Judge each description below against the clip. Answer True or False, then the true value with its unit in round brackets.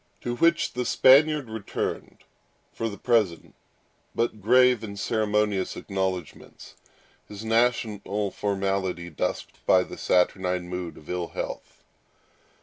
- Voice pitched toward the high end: False (105 Hz)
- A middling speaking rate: False (115 wpm)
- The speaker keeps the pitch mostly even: False (4.0 semitones)